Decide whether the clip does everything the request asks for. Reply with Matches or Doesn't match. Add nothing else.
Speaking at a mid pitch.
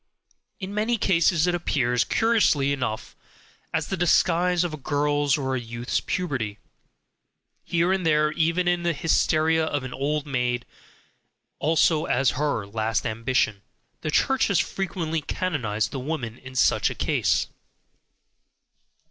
Matches